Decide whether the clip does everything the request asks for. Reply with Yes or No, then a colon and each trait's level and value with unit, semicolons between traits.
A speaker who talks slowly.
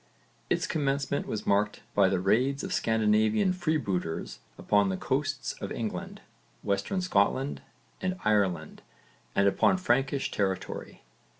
Yes: slow, 120 wpm